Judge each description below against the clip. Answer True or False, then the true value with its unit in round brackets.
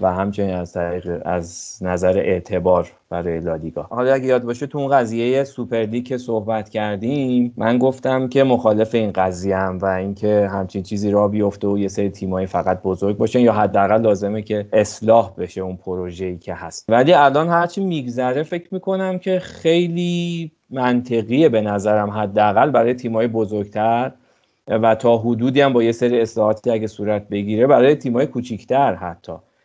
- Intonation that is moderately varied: True (4.4 semitones)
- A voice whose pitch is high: False (110 Hz)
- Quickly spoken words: True (160 wpm)